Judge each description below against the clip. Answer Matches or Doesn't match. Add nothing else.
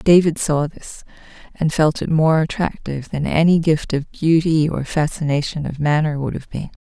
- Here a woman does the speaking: Matches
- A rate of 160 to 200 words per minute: Matches